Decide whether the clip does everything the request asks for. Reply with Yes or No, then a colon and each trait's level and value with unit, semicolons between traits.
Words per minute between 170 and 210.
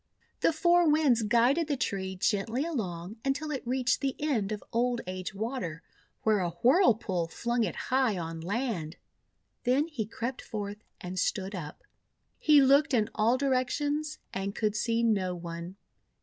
No: average, 155 wpm